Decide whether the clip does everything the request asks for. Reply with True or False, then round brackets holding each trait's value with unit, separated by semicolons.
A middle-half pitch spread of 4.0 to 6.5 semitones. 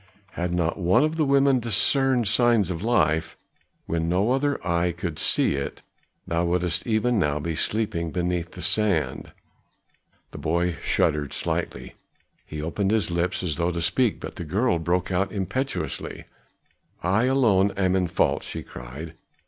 True (4.8 semitones)